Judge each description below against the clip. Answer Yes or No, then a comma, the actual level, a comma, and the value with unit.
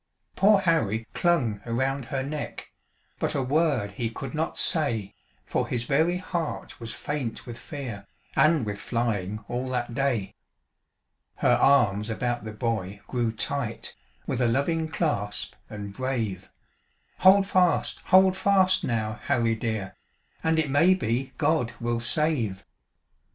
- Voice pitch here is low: Yes, low, 125 Hz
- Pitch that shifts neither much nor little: No, wide, 5.9 semitones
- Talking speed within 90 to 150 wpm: Yes, average, 140 wpm